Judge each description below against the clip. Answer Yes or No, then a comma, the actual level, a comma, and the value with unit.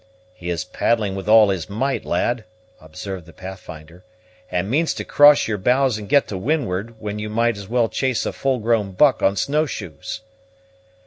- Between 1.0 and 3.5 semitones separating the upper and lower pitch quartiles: No, average, 4.6 semitones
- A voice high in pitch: No, low, 110 Hz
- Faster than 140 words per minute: Yes, average, 185 wpm